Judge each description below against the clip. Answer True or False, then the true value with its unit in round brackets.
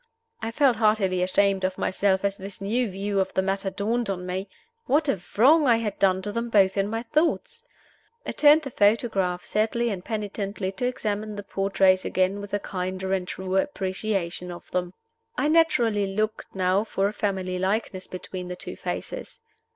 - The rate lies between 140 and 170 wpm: False (180 wpm)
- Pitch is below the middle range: False (200 Hz)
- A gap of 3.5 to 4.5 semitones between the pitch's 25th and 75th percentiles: False (3.0 semitones)